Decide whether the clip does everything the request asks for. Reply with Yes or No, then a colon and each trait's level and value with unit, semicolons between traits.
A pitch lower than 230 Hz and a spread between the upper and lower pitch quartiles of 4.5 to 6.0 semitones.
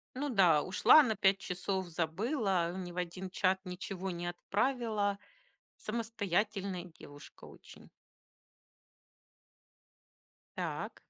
No: high, 190 Hz; average, 3.1 semitones